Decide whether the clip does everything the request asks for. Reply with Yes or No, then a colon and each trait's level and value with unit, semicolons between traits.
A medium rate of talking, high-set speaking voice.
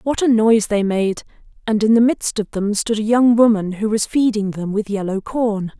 No: fast, 230 wpm; high, 215 Hz